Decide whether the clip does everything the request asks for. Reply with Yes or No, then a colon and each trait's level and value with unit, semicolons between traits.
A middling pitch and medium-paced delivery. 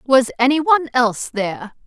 No: very high, 255 Hz; average, 160 wpm